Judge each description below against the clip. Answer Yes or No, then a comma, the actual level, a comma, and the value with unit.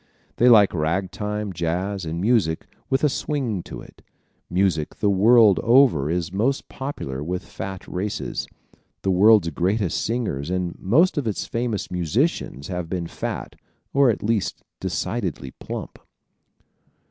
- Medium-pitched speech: No, very low, 95 Hz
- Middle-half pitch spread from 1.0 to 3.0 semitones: No, average, 5.0 semitones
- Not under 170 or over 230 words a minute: No, slow, 135 wpm